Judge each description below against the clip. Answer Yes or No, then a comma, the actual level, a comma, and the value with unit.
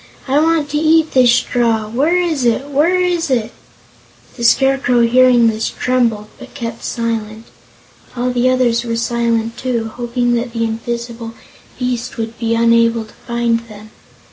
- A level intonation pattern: Yes, narrow, 1.9 semitones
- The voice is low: No, high, 235 Hz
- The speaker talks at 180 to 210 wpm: No, average, 155 wpm